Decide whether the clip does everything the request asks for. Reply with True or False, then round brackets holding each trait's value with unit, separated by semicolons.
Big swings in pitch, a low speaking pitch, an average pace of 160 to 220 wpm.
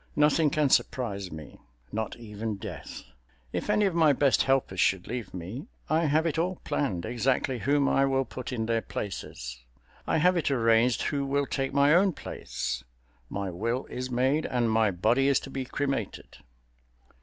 True (5.9 semitones; 125 Hz; 165 wpm)